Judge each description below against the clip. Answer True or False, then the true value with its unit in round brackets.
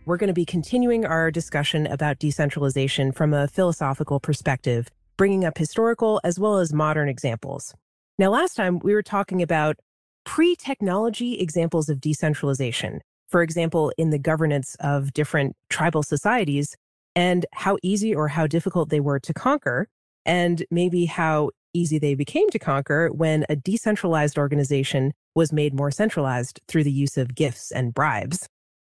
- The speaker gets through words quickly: False (155 wpm)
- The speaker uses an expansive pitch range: False (3.9 semitones)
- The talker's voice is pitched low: False (155 Hz)